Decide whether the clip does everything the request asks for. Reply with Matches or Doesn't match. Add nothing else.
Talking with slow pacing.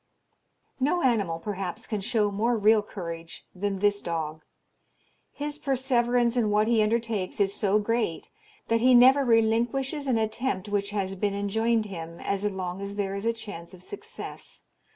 Doesn't match